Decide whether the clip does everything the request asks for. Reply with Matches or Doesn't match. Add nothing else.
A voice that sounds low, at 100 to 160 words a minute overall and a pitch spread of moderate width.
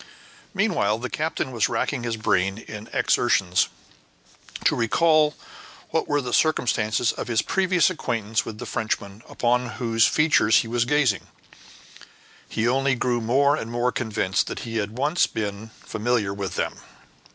Matches